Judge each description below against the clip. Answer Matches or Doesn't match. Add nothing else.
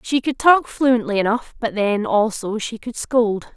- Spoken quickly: Doesn't match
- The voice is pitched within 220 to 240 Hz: Matches